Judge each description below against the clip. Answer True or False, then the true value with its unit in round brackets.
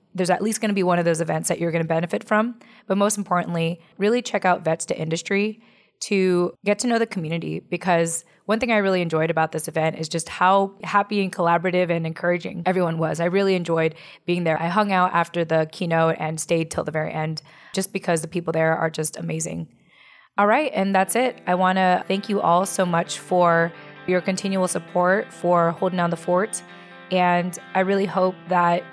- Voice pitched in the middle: True (175 Hz)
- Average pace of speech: False (210 wpm)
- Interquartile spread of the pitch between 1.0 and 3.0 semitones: True (2.7 semitones)